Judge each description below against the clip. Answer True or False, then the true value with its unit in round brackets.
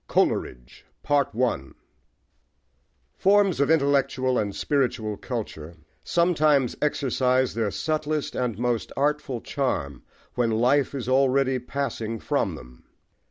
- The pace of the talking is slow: True (100 wpm)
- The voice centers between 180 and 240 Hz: False (130 Hz)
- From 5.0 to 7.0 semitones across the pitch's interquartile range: False (3.8 semitones)